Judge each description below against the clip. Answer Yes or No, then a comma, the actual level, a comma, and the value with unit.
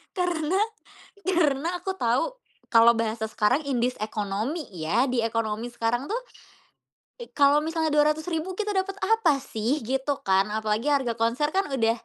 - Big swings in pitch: Yes, wide, 6.0 semitones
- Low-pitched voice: No, very high, 270 Hz